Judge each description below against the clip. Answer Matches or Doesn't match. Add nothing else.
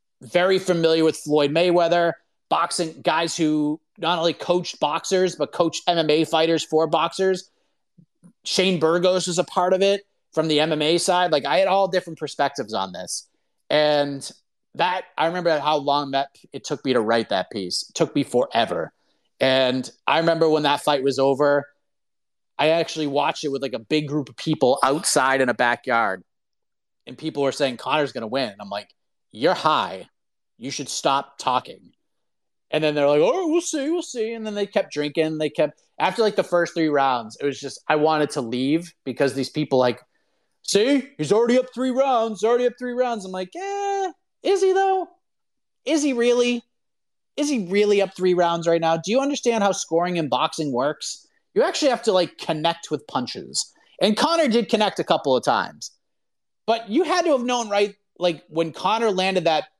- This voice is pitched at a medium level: Matches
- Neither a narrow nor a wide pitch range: Doesn't match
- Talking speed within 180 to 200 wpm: Matches